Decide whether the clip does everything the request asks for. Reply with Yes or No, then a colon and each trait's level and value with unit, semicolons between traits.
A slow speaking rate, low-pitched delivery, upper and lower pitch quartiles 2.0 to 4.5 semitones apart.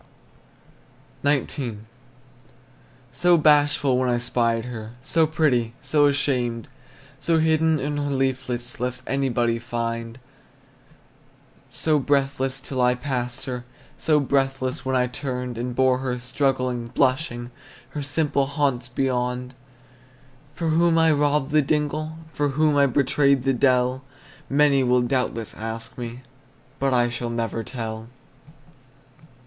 Yes: slow, 120 wpm; low, 130 Hz; average, 2.9 semitones